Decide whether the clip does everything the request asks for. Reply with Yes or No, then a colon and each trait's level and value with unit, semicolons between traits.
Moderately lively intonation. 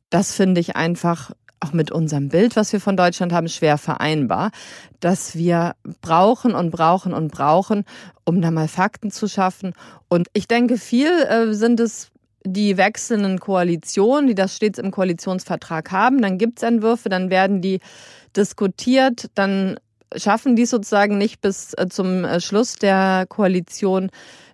Yes: average, 3.8 semitones